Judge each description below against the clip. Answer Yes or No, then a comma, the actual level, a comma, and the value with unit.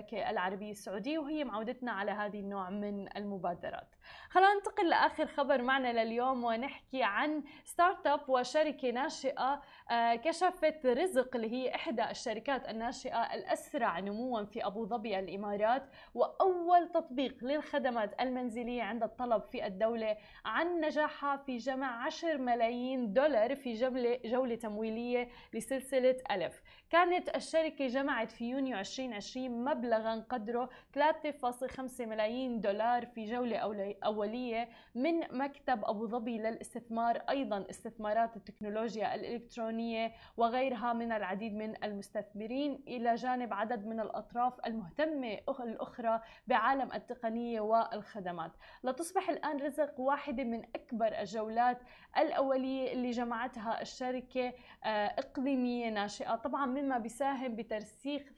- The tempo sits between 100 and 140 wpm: Yes, average, 115 wpm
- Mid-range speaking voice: No, high, 245 Hz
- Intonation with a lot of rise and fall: No, average, 3.6 semitones